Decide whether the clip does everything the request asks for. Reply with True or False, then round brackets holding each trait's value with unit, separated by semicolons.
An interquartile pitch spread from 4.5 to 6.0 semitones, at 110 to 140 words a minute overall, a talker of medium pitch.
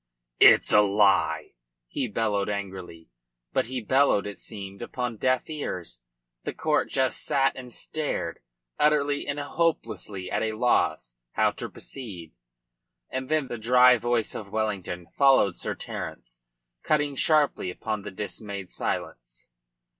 False (5.2 semitones; 135 wpm; 110 Hz)